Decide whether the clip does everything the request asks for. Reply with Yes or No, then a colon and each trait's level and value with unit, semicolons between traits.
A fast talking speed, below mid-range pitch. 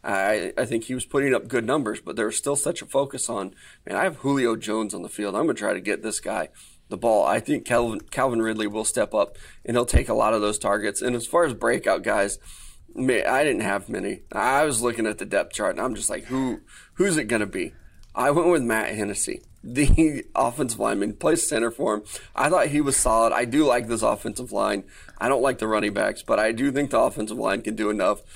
Yes: fast, 240 wpm; low, 120 Hz